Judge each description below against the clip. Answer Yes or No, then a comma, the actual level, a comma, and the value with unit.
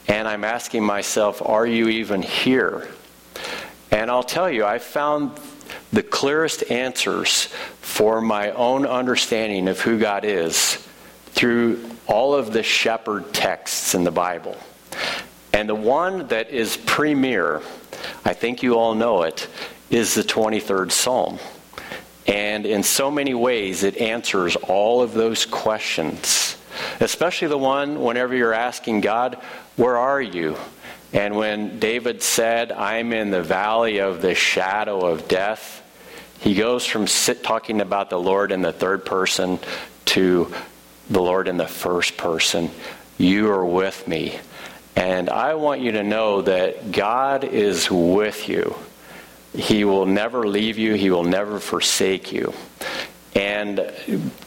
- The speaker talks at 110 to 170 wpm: Yes, average, 140 wpm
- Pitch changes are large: No, average, 3.3 semitones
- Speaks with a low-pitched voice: Yes, low, 110 Hz